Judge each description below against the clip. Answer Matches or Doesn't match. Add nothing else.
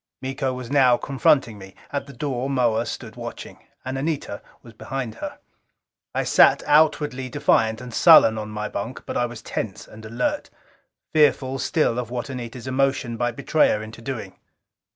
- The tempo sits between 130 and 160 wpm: Doesn't match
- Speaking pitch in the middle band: Doesn't match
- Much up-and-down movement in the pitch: Doesn't match